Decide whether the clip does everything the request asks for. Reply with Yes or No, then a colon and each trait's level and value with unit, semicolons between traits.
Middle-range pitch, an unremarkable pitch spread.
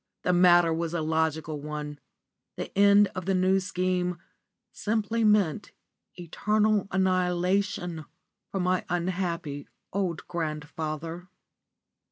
Yes: medium, 180 Hz; average, 3.0 semitones